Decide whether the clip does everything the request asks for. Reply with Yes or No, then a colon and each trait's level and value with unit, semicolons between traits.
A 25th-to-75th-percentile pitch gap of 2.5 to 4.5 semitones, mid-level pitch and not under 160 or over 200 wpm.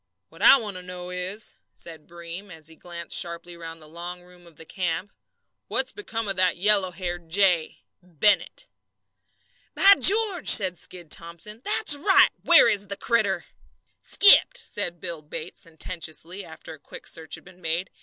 Yes: average, 3.3 semitones; medium, 180 Hz; average, 165 wpm